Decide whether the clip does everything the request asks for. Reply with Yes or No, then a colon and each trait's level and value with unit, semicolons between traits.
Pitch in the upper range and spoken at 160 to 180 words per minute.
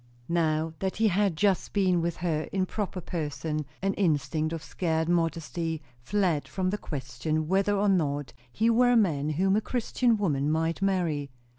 No: medium, 170 Hz; average, 170 wpm